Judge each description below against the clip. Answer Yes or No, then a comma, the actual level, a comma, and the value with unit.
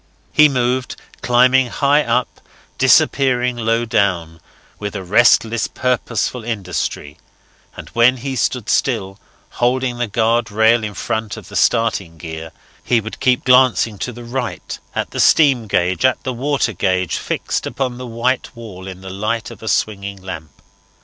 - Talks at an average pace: Yes, average, 155 wpm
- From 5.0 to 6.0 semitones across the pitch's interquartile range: No, average, 4.0 semitones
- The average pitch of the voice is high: No, low, 115 Hz